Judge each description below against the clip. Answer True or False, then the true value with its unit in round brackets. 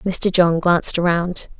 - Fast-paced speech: False (150 wpm)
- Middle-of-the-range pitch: True (175 Hz)